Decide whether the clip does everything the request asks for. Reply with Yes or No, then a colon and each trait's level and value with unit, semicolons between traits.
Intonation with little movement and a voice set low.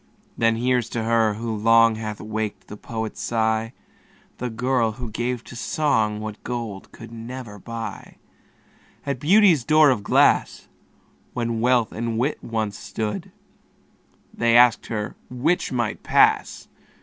Yes: narrow, 2.0 semitones; low, 115 Hz